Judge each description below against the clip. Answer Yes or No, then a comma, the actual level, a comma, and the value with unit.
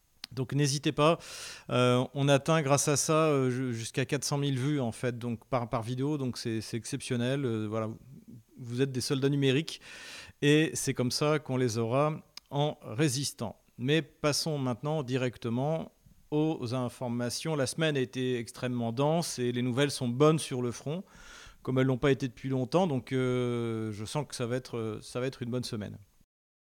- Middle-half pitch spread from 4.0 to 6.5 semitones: No, average, 3.2 semitones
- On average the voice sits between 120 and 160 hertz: Yes, low, 130 Hz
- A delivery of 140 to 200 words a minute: Yes, average, 180 wpm